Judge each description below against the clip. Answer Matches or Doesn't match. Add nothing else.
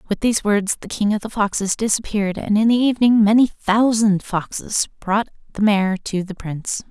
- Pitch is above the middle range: Matches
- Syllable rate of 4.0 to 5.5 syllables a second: Matches